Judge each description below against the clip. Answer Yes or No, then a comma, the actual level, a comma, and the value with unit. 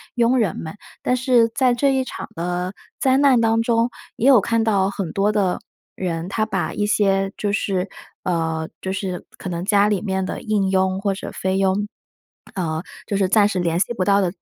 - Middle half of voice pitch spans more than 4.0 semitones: No, average, 3.2 semitones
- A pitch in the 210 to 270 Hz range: No, high, 200 Hz